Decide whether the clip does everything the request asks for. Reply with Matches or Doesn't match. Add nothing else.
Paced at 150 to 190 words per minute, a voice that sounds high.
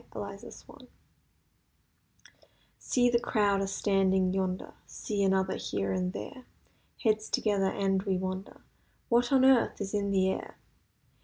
Doesn't match